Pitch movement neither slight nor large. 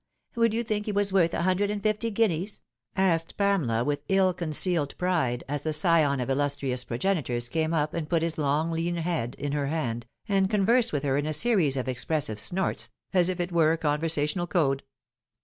Yes: average, 4.8 semitones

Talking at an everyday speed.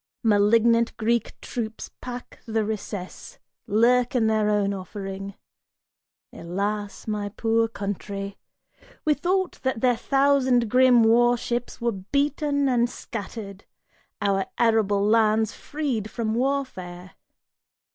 No: slow, 110 wpm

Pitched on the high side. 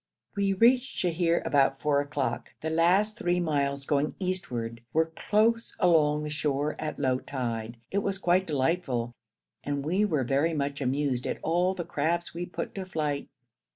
No: medium, 155 Hz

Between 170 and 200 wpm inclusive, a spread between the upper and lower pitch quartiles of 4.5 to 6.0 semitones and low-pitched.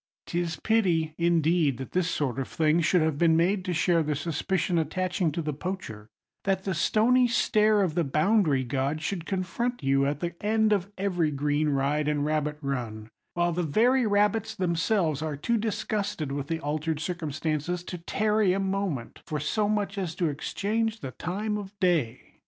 No: average, 180 wpm; average, 4.9 semitones; medium, 170 Hz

